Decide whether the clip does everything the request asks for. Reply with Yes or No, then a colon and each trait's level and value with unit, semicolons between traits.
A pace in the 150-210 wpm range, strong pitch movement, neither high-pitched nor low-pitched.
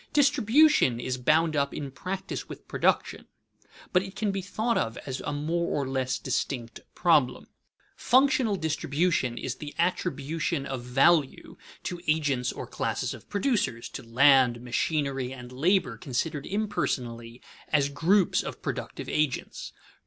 No: average, 140 wpm; wide, 6.0 semitones; medium, 145 Hz